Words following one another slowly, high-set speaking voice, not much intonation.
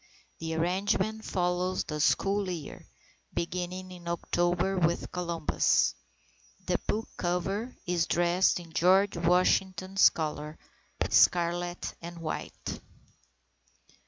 No: slow, 100 wpm; medium, 175 Hz; narrow, 1.7 semitones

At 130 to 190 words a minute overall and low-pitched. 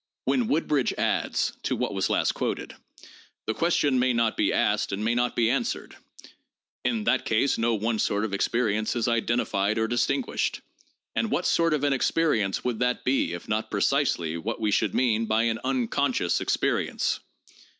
Yes: average, 175 wpm; low, 115 Hz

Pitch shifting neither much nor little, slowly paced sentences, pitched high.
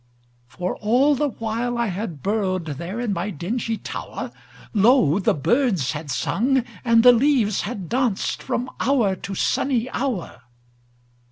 Yes: average, 4.9 semitones; slow, 125 wpm; high, 220 Hz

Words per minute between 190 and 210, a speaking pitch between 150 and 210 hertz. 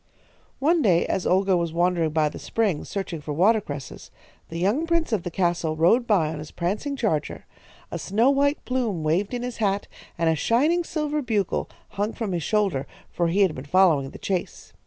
Yes: average, 195 wpm; high, 190 Hz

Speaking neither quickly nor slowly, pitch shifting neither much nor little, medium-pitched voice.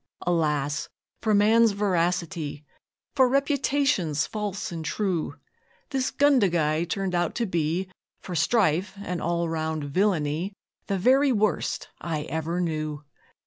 No: slow, 120 wpm; average, 4.8 semitones; medium, 180 Hz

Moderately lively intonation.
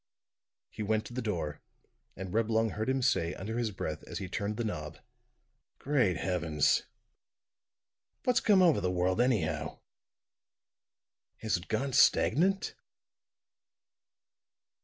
No: wide, 5.7 semitones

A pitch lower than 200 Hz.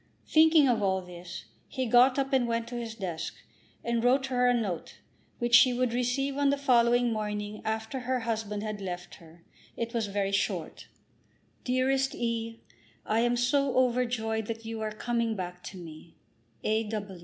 No: high, 230 Hz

